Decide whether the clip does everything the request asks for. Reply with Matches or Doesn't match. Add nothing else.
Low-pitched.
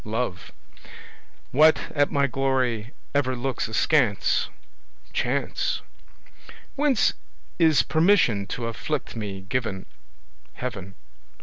Matches